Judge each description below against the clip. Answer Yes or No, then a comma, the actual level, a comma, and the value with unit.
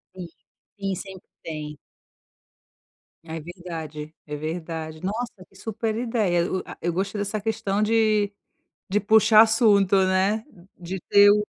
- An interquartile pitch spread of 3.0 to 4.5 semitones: Yes, average, 3.9 semitones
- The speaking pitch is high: Yes, high, 195 Hz